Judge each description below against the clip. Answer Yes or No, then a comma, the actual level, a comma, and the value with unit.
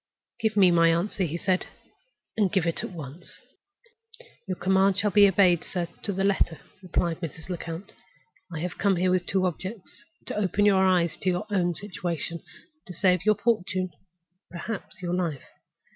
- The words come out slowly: No, average, 170 wpm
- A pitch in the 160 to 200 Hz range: Yes, medium, 185 Hz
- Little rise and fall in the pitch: Yes, narrow, 2.3 semitones